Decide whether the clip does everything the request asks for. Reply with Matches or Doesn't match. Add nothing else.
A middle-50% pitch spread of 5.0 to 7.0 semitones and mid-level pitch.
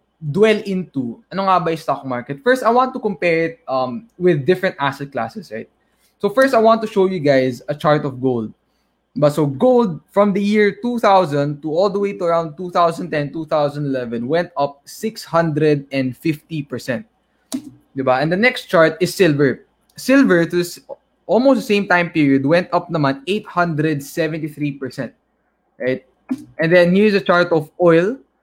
Matches